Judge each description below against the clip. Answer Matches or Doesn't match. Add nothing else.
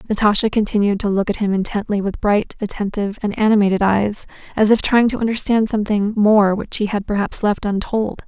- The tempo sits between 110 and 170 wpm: Doesn't match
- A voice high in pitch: Matches